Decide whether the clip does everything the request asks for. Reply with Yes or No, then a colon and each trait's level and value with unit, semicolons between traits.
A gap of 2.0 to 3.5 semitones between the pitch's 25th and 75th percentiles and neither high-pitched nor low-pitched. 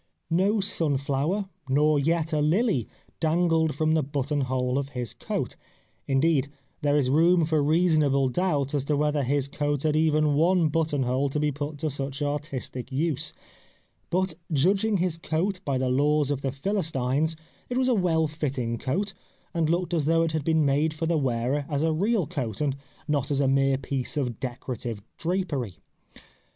Yes: average, 3.2 semitones; medium, 150 Hz